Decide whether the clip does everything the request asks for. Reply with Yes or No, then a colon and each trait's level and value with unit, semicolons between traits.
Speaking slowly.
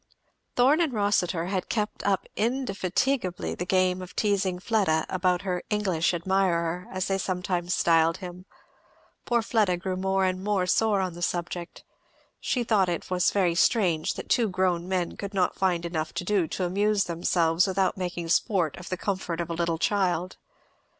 No: average, 170 wpm